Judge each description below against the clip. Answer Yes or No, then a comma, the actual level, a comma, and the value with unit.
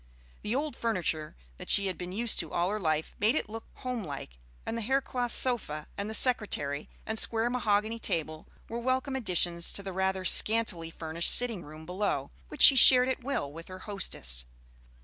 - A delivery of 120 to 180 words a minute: No, average, 190 wpm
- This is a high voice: Yes, high, 205 Hz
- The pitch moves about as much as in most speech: No, wide, 6.2 semitones